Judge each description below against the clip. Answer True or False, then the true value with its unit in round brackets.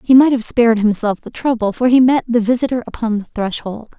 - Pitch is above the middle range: True (235 Hz)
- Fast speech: True (225 wpm)